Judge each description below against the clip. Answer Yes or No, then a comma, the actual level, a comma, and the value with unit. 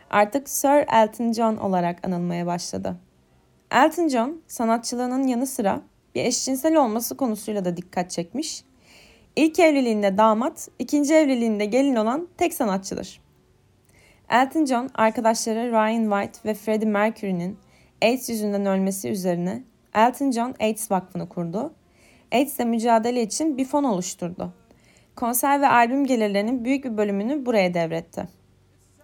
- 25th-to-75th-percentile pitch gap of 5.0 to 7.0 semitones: Yes, average, 5.3 semitones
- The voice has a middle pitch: No, high, 225 Hz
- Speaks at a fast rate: No, average, 125 wpm